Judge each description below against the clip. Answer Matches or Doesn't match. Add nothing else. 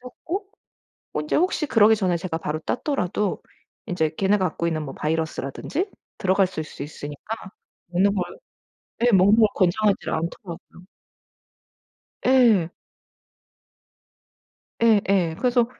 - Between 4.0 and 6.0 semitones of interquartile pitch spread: Matches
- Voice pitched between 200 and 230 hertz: Doesn't match